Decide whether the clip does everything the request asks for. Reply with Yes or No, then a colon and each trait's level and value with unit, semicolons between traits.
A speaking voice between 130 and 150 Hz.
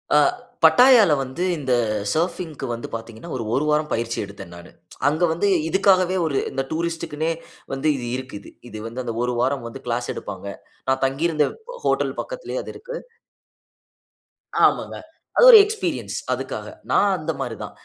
Yes: medium, 140 Hz